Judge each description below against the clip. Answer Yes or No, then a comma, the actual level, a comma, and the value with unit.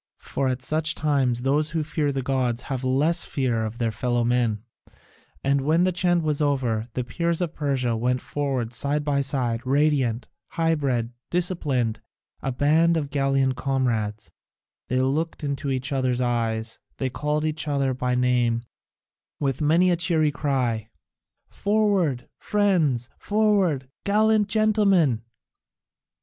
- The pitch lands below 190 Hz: Yes, low, 135 Hz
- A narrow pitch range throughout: No, average, 4.1 semitones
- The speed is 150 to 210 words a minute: No, average, 140 wpm